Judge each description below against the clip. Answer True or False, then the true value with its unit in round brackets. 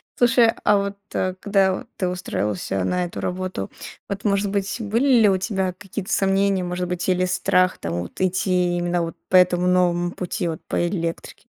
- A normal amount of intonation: False (2.0 semitones)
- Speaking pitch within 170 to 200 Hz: True (185 Hz)